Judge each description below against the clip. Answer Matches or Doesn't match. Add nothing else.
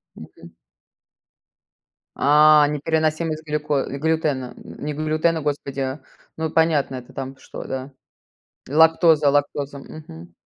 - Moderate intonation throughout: Doesn't match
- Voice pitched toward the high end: Doesn't match